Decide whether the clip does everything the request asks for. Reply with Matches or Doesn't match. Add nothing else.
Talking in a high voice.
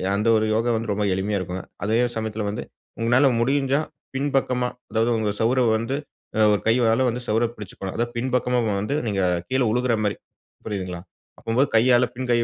Doesn't match